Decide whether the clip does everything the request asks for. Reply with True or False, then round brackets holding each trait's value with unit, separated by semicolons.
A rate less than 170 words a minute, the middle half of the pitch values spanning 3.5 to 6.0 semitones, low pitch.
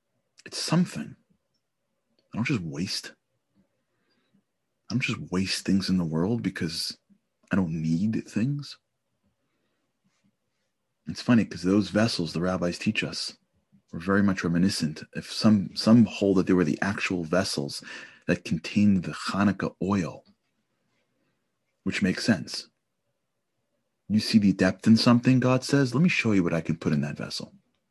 True (150 wpm; 4.6 semitones; 95 Hz)